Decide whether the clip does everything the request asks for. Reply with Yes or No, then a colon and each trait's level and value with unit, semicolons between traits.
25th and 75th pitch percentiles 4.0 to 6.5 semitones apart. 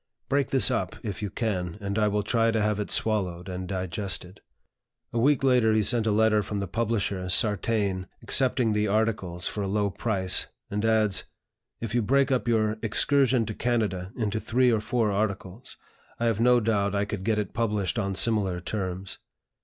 No: narrow, 2.6 semitones